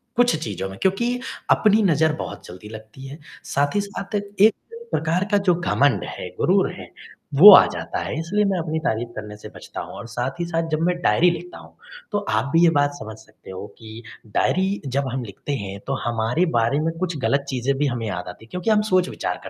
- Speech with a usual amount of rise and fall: No, wide, 8.3 semitones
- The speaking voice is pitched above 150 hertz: No, medium, 145 Hz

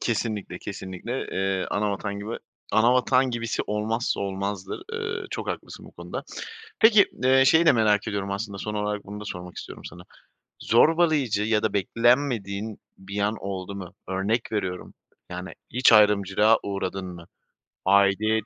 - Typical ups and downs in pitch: Yes, average, 3.0 semitones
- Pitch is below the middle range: Yes, low, 105 Hz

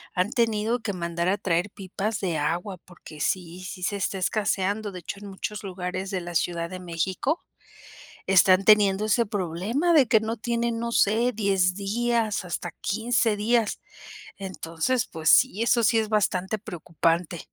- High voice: Yes, high, 195 Hz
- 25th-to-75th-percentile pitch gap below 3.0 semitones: No, average, 3.6 semitones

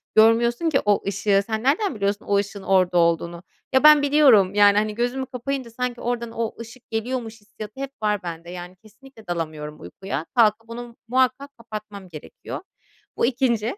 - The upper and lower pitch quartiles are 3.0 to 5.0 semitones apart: Yes, average, 4.0 semitones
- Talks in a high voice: Yes, high, 220 Hz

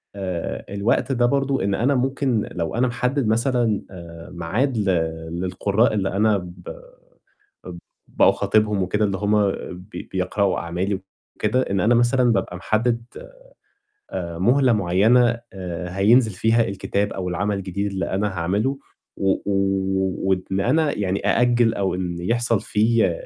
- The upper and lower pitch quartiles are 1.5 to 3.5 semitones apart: No, average, 4.0 semitones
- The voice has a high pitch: No, low, 100 Hz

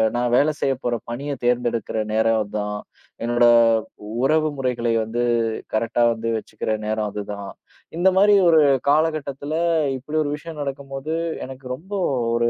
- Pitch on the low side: Yes, low, 125 Hz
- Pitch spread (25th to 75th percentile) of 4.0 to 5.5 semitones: Yes, average, 4.3 semitones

